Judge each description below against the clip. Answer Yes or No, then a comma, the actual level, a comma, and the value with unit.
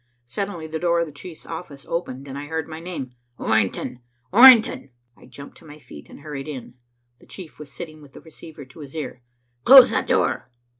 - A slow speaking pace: No, average, 200 wpm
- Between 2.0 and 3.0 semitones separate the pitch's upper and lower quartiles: No, average, 3.5 semitones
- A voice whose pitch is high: No, medium, 155 Hz